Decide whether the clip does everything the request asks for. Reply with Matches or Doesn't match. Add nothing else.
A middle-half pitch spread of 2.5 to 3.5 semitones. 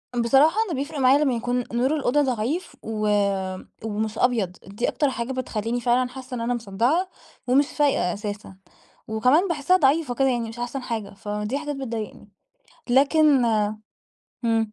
Doesn't match